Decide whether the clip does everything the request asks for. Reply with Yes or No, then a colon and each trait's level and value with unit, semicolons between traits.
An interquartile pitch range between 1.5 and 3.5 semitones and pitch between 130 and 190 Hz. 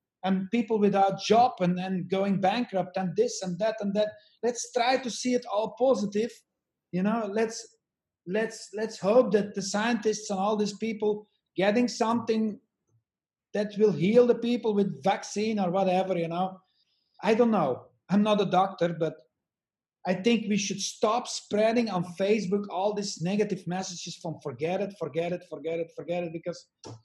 No: average, 3.2 semitones; high, 205 Hz